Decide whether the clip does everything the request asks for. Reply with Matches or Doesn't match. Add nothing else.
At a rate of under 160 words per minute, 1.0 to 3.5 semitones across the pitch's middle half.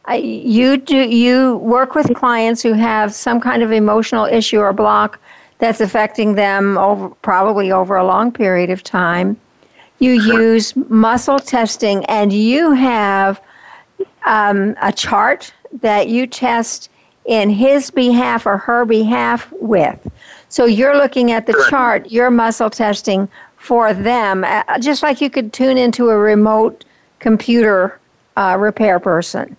Matches